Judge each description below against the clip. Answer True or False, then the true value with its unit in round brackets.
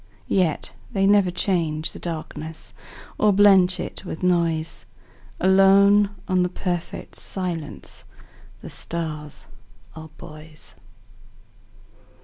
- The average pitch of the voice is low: False (180 Hz)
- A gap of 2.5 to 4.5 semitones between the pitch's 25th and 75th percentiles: True (3.3 semitones)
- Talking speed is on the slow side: True (85 wpm)